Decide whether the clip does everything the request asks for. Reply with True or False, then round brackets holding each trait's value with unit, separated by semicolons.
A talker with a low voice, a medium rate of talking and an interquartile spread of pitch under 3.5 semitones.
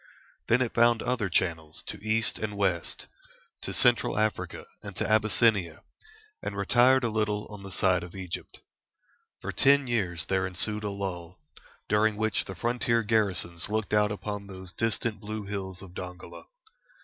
True (105 Hz; 160 wpm; 2.8 semitones)